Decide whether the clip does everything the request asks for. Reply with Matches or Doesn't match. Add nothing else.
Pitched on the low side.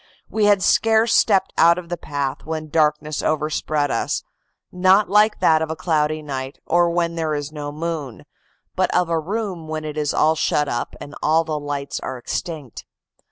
Doesn't match